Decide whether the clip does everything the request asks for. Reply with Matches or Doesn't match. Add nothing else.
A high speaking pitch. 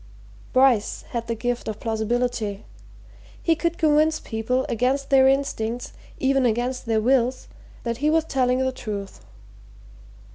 Matches